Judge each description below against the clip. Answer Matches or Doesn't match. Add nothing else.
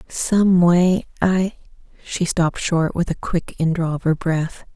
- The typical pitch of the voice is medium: Matches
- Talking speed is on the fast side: Doesn't match